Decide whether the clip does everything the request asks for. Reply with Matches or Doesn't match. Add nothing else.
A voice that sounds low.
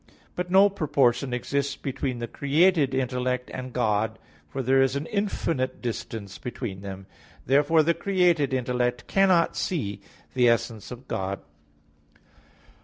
Matches